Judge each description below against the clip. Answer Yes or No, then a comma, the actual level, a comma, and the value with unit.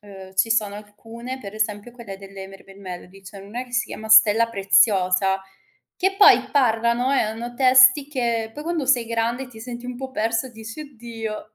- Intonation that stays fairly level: No, average, 3.4 semitones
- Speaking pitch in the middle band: No, high, 225 Hz